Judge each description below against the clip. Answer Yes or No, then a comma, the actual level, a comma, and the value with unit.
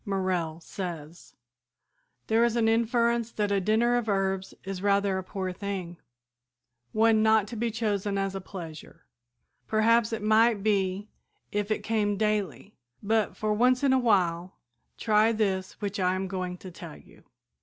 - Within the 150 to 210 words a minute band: Yes, average, 160 wpm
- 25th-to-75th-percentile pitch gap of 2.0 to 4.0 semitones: Yes, average, 2.8 semitones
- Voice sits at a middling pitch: No, high, 205 Hz